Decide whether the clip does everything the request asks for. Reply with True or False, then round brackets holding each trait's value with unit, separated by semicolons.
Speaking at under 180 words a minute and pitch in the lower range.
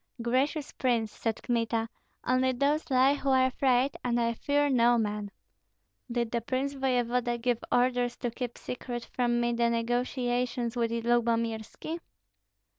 False (140 wpm; 245 Hz)